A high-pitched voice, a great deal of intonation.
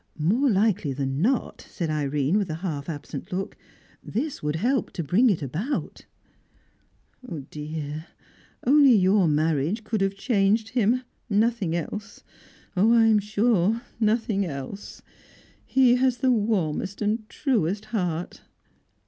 Yes: high, 200 Hz; wide, 6.2 semitones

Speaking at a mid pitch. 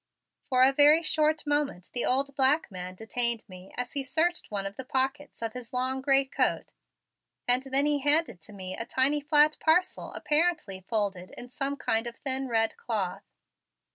No: very high, 260 Hz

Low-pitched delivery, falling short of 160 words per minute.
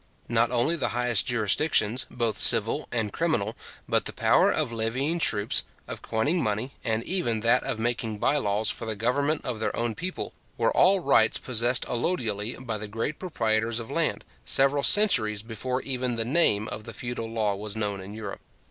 No: low, 115 Hz; average, 185 wpm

